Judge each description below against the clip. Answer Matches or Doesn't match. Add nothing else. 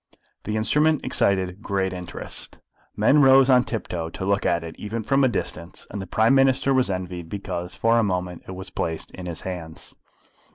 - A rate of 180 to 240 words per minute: Matches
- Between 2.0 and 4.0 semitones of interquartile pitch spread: Doesn't match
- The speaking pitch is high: Doesn't match